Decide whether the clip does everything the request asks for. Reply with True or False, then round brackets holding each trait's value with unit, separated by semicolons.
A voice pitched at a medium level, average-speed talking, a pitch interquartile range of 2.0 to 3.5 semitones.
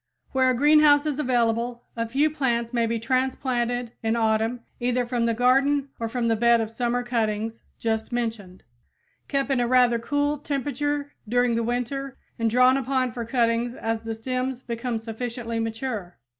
False (240 Hz; 170 wpm; 2.4 semitones)